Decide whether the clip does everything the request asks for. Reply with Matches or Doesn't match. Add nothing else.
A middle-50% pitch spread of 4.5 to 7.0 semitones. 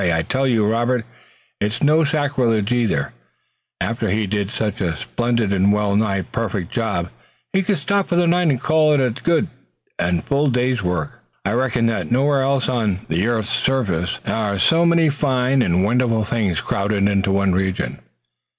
Matches